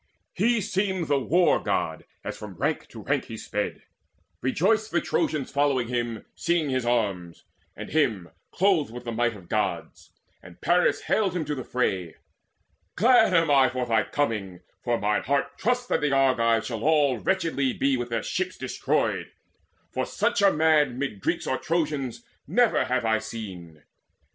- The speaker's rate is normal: Yes, average, 170 wpm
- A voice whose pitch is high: No, low, 135 Hz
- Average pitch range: No, wide, 6.2 semitones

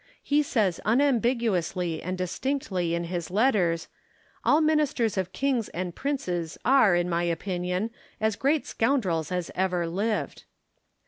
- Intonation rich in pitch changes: Yes, wide, 6.6 semitones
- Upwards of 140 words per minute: No, slow, 135 wpm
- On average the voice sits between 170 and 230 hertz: Yes, high, 190 Hz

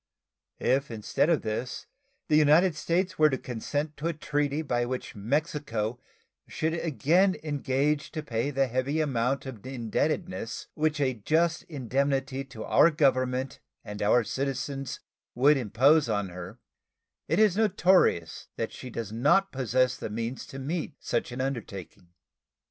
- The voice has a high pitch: No, low, 135 Hz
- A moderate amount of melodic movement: Yes, average, 4.1 semitones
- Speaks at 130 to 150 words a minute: Yes, average, 145 wpm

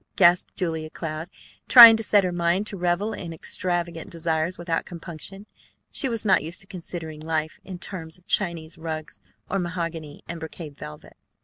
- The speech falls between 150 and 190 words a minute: Yes, average, 170 wpm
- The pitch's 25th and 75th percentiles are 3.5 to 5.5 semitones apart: No, narrow, 2.5 semitones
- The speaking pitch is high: No, medium, 170 Hz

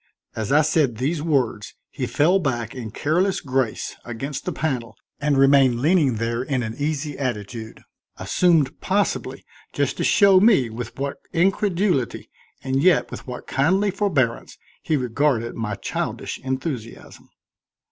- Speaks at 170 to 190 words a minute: No, average, 140 wpm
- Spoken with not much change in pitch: No, average, 5.2 semitones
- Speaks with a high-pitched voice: No, low, 135 Hz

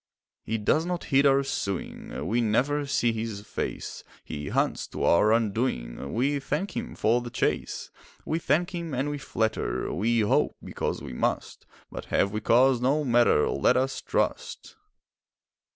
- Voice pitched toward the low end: Yes, low, 120 Hz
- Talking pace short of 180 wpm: Yes, average, 155 wpm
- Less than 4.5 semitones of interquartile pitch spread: No, average, 4.9 semitones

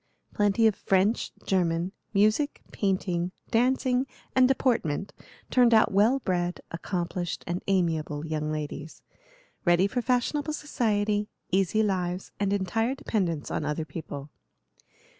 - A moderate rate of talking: No, slow, 120 wpm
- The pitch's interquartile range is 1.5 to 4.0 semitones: No, average, 4.7 semitones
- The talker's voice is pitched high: Yes, high, 195 Hz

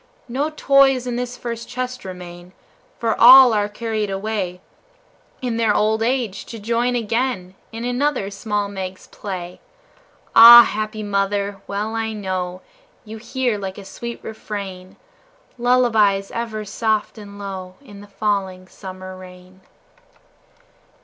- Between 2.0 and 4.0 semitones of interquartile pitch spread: Yes, average, 3.5 semitones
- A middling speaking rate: No, slow, 130 wpm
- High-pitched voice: Yes, high, 210 Hz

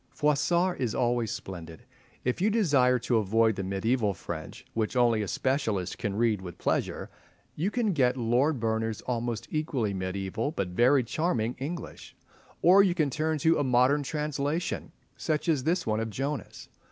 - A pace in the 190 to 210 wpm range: No, average, 165 wpm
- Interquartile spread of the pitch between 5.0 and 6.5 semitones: Yes, average, 5.3 semitones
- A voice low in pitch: Yes, low, 125 Hz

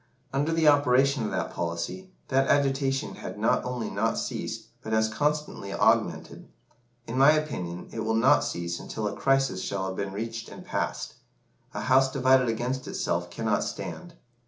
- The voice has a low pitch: Yes, low, 125 Hz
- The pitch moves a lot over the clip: No, average, 4.2 semitones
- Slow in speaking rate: No, average, 165 wpm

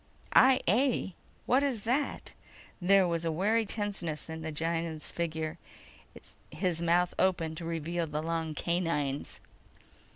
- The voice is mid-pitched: Yes, medium, 170 Hz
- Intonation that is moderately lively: Yes, average, 3.3 semitones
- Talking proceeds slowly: Yes, slow, 130 wpm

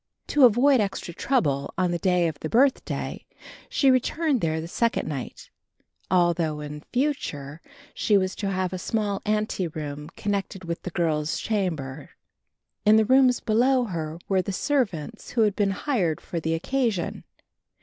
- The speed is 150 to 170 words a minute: Yes, average, 160 wpm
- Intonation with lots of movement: Yes, wide, 6.2 semitones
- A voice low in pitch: No, high, 190 Hz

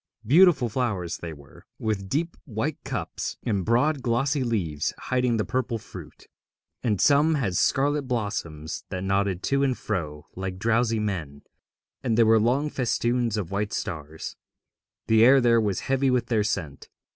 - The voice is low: Yes, low, 115 Hz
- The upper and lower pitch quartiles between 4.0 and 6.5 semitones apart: Yes, average, 5.1 semitones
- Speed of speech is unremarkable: Yes, average, 155 wpm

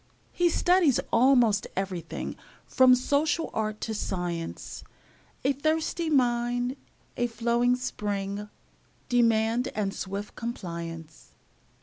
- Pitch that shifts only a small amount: No, average, 4.2 semitones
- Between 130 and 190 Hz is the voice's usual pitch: No, high, 235 Hz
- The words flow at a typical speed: No, slow, 95 wpm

